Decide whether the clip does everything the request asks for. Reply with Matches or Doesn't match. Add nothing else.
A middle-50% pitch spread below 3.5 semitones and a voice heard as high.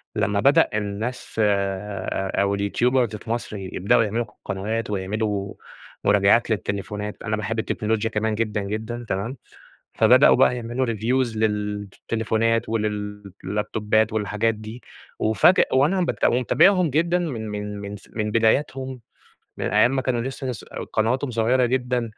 Doesn't match